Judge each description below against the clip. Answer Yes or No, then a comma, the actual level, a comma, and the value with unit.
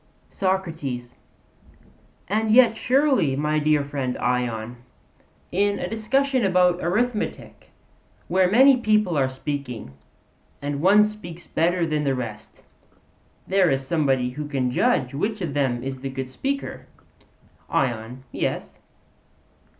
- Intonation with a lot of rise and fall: Yes, wide, 7.5 semitones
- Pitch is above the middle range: No, medium, 155 Hz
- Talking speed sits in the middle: No, slow, 120 wpm